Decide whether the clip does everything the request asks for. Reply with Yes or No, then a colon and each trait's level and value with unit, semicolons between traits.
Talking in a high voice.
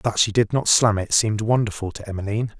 No: low, 110 Hz